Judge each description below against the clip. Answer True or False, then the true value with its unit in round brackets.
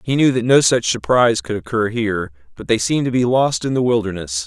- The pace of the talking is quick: True (240 wpm)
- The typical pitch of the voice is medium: False (110 Hz)